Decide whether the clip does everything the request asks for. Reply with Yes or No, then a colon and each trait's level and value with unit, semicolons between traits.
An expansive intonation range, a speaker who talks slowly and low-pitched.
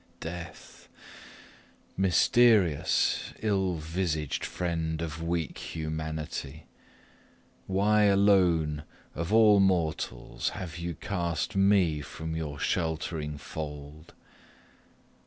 No: average, 3.5 semitones; slow, 85 wpm; very low, 85 Hz